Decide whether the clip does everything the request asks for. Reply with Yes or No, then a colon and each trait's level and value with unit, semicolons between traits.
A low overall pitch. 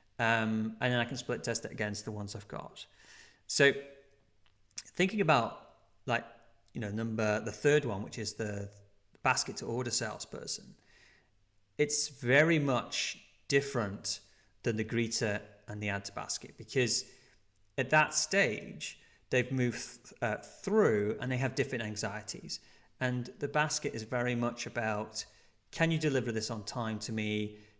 Yes: low, 115 Hz